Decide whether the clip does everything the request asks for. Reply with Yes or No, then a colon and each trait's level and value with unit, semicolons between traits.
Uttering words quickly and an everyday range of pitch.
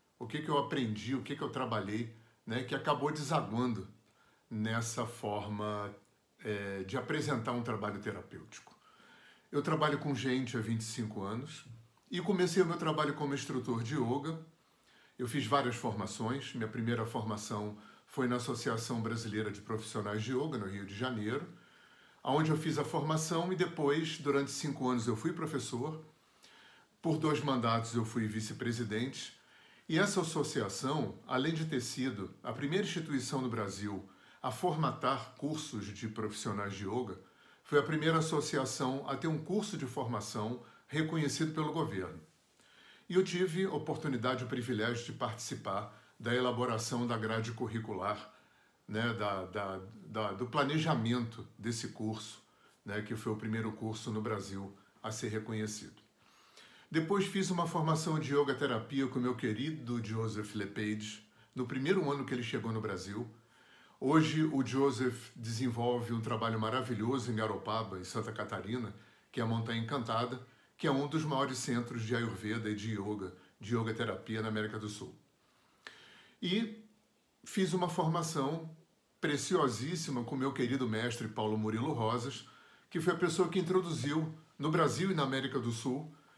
No: average, 155 wpm; average, 5.0 semitones